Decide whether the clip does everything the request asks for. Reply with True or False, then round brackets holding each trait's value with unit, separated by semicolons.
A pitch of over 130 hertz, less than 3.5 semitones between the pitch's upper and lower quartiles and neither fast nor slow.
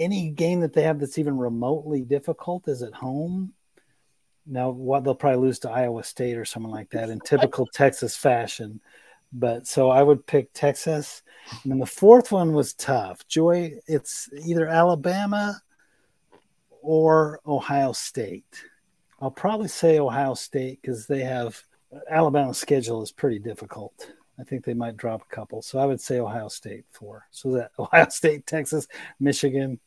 False (140 Hz; 3.9 semitones; 160 wpm)